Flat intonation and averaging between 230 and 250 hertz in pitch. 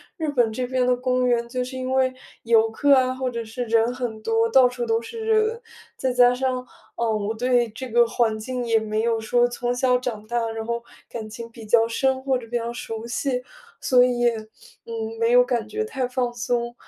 Yes: narrow, 1.9 semitones; high, 240 Hz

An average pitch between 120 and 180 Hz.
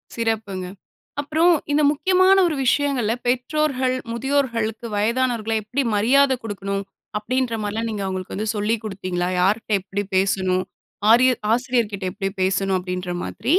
No: high, 225 Hz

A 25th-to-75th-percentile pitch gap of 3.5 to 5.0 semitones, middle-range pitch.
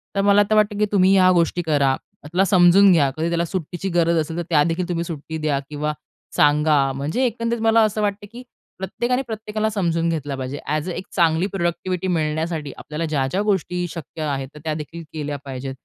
Yes: average, 4.4 semitones; medium, 170 Hz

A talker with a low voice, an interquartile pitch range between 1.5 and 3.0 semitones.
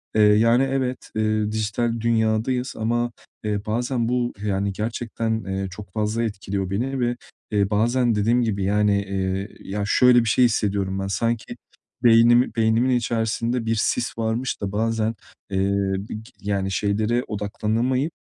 Yes: low, 110 Hz; narrow, 2.6 semitones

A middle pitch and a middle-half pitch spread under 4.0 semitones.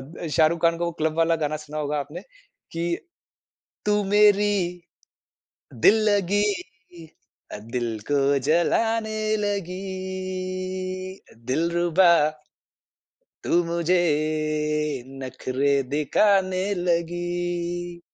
Yes: medium, 175 Hz; average, 3.4 semitones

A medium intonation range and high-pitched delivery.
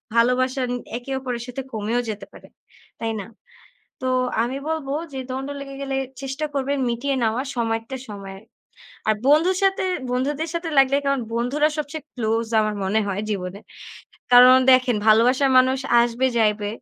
Yes: average, 3.4 semitones; very high, 255 Hz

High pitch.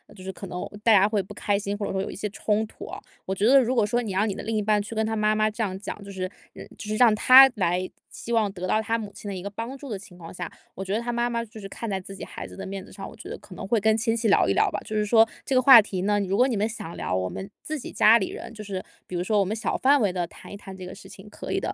Yes: high, 210 Hz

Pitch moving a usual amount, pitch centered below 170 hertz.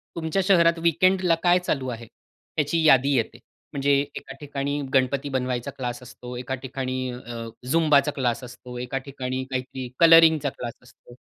Yes: average, 3.8 semitones; low, 135 Hz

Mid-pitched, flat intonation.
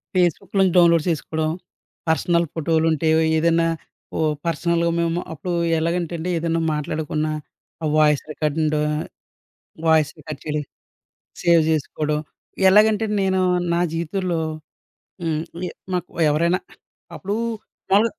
Yes: medium, 165 Hz; narrow, 2.1 semitones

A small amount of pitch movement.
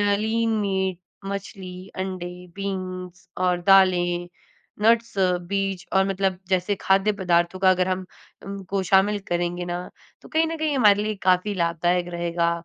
Yes: narrow, 1.9 semitones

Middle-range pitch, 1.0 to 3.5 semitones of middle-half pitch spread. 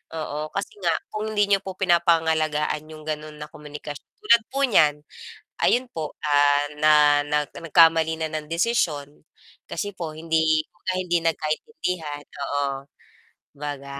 Yes: medium, 155 Hz; narrow, 2.5 semitones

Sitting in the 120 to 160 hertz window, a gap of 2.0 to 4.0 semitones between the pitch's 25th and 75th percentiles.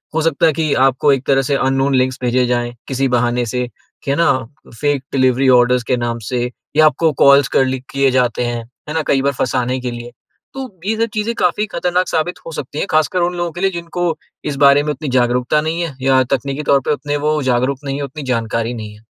Yes: low, 135 Hz; average, 3.7 semitones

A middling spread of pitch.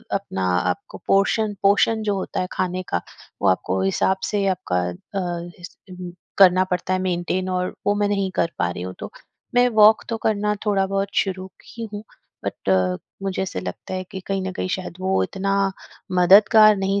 No: narrow, 2.1 semitones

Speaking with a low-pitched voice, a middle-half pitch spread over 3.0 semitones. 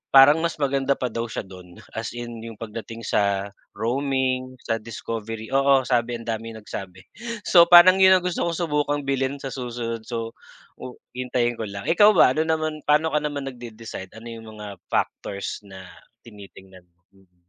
Yes: low, 120 Hz; average, 4.1 semitones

